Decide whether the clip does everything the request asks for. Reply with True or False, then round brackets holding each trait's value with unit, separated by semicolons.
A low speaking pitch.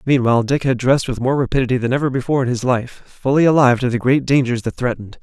True (130 Hz)